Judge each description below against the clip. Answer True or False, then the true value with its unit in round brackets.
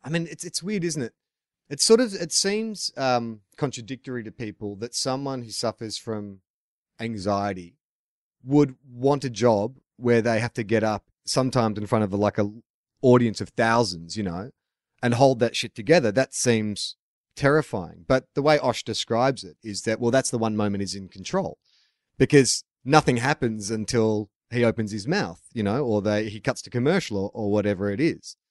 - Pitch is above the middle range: False (115 Hz)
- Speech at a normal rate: True (185 wpm)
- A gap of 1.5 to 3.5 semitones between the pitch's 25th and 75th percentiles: False (4.0 semitones)